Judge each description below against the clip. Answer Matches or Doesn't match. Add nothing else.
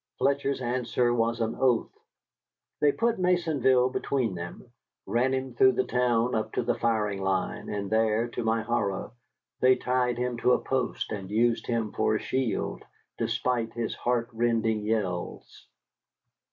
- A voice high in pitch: Doesn't match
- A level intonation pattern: Matches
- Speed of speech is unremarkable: Matches